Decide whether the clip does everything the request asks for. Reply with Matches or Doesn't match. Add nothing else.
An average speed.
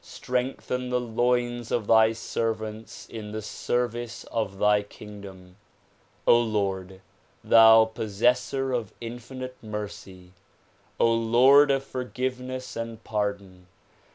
Doesn't match